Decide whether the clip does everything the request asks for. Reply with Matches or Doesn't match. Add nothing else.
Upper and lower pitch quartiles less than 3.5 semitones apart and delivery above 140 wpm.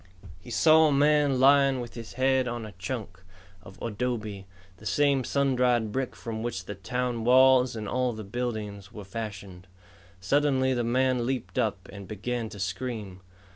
Doesn't match